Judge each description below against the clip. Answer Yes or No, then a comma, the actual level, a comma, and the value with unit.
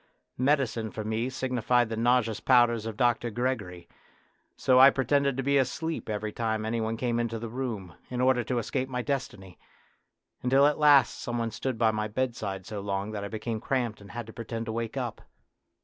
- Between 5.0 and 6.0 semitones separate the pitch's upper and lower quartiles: No, average, 2.7 semitones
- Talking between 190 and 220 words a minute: Yes, average, 195 wpm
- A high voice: No, low, 120 Hz